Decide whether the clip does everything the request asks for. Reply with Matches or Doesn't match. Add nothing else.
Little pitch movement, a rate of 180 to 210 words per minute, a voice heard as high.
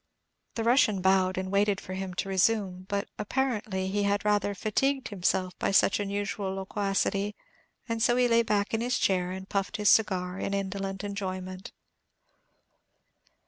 Doesn't match